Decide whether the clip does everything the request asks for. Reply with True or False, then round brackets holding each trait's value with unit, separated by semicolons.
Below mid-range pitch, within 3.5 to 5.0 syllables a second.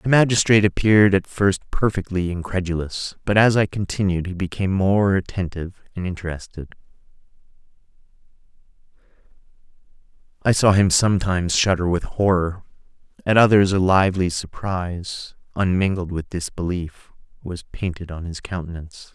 False (95 Hz; 5.4 syllables/s)